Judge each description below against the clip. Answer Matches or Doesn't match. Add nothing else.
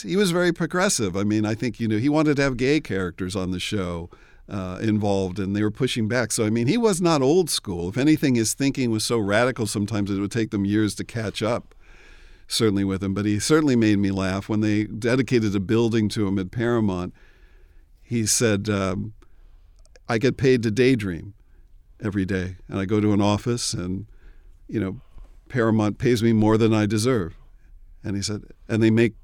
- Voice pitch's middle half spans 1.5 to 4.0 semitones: Matches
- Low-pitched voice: Matches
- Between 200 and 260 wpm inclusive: Matches